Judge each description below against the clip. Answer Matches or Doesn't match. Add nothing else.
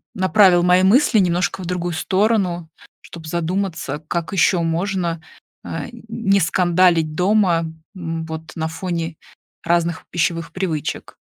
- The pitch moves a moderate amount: Doesn't match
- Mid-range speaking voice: Matches